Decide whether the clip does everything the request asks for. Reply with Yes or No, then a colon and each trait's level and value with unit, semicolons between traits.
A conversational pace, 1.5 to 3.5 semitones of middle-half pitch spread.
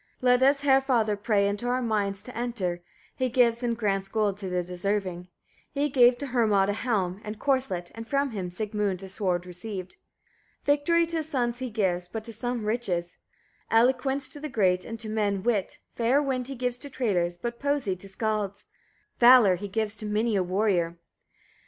No: average, 190 wpm; average, 4.3 semitones